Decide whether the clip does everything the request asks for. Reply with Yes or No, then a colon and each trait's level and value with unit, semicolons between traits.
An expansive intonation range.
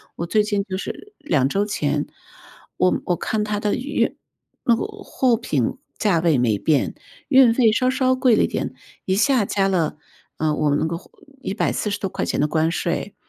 Yes: wide, 6.8 semitones